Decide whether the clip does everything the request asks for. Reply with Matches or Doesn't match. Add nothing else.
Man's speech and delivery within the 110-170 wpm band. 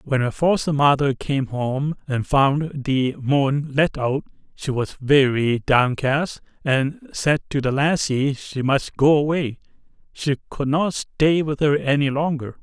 Matches